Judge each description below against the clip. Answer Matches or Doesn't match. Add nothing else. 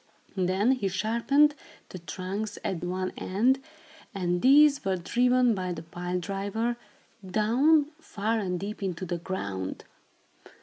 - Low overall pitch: Doesn't match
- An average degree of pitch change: Matches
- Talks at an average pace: Doesn't match